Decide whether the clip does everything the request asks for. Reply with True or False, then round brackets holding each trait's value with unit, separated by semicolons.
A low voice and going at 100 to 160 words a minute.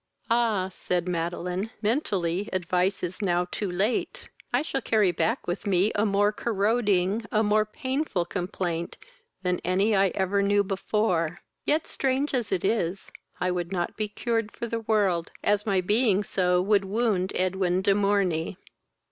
False (195 Hz; 155 wpm)